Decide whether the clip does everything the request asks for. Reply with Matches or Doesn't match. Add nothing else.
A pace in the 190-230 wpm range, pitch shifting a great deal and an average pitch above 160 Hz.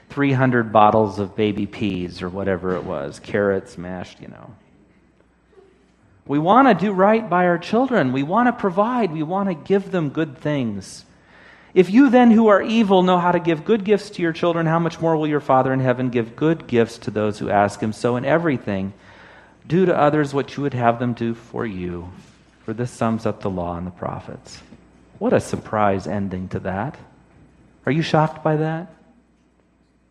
Doesn't match